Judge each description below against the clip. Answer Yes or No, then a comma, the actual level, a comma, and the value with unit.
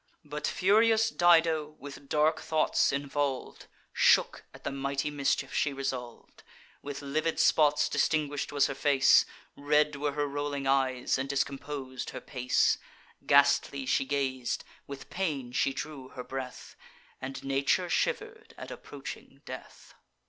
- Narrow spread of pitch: Yes, narrow, 1.8 semitones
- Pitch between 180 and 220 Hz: No, medium, 140 Hz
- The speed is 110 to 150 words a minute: Yes, slow, 135 wpm